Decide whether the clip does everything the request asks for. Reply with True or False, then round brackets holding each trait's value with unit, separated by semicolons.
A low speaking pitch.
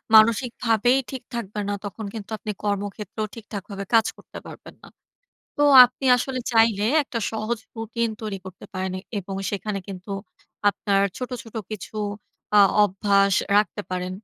False (210 Hz)